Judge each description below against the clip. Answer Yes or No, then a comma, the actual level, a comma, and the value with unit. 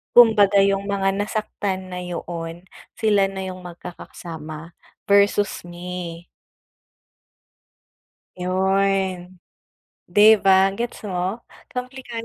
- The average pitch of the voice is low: No, high, 190 Hz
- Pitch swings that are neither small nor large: No, narrow, 2.3 semitones